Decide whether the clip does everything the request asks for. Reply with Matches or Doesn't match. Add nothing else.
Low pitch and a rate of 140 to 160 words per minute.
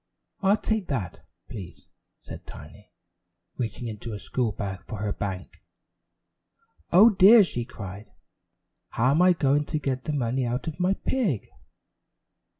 Matches